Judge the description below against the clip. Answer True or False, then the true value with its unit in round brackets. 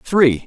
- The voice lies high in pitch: False (140 Hz)